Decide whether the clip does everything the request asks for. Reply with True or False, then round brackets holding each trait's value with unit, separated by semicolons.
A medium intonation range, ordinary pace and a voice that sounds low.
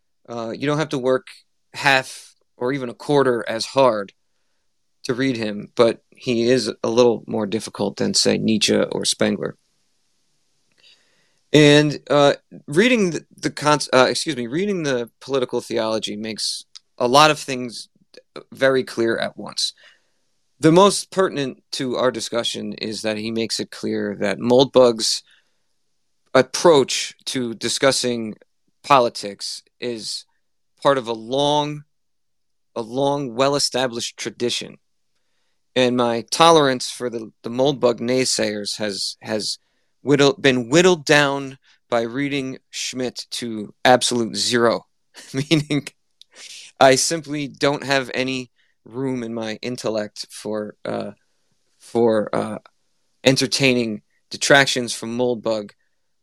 False (3.6 semitones; 125 wpm; 125 Hz)